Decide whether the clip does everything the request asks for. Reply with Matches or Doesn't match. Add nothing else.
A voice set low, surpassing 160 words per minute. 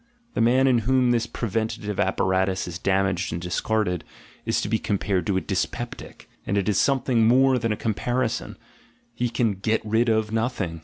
Matches